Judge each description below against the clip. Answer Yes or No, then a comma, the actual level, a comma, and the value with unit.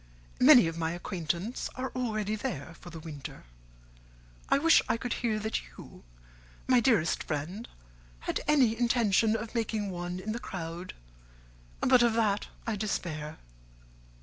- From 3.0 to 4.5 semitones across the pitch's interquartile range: No, wide, 5.5 semitones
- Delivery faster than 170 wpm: No, average, 145 wpm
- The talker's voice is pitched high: Yes, high, 215 Hz